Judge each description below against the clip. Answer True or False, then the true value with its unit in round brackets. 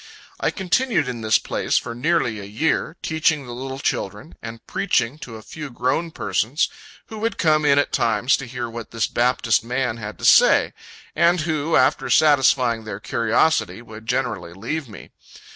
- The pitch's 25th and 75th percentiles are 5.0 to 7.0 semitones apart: True (5.4 semitones)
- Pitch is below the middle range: True (125 Hz)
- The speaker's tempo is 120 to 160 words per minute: False (175 wpm)